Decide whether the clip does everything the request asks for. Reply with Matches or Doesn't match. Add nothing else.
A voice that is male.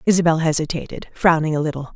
Doesn't match